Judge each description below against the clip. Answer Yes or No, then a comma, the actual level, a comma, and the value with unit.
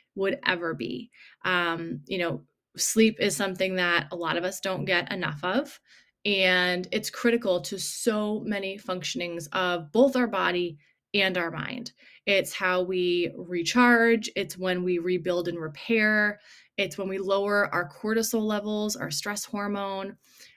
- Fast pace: No, average, 150 wpm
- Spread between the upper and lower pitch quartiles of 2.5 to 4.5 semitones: Yes, average, 2.8 semitones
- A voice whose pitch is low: No, high, 190 Hz